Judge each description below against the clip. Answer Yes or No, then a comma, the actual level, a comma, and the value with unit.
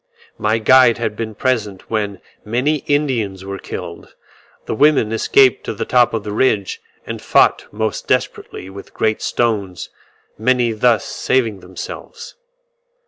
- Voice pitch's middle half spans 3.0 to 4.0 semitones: Yes, average, 3.5 semitones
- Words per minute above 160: No, average, 140 wpm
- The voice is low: Yes, low, 110 Hz